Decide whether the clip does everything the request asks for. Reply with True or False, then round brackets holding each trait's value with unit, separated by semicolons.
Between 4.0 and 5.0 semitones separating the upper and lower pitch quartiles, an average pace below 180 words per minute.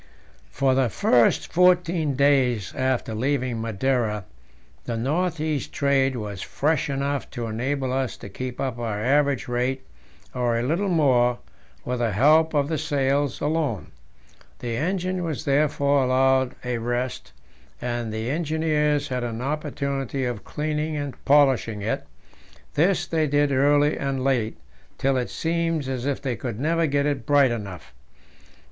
False (3.4 semitones; 150 wpm)